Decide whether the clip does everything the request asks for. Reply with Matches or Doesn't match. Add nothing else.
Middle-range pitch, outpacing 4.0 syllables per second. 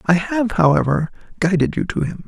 Matches